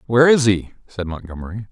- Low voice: Yes, low, 105 Hz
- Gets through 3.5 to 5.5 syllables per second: No, 6.4 syllables/s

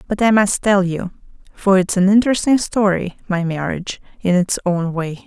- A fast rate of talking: No, average, 180 wpm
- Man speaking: No, female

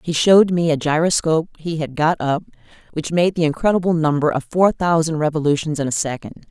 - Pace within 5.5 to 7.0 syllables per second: Yes, 6.0 syllables/s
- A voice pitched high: No, medium, 160 Hz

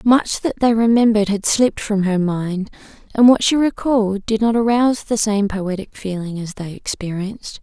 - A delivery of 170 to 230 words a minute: Yes, average, 180 wpm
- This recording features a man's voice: No, female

